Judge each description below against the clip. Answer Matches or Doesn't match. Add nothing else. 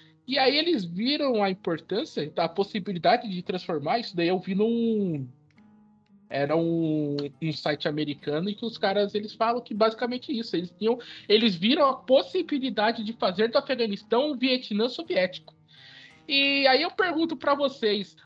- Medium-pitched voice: Doesn't match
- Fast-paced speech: Doesn't match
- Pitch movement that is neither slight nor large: Doesn't match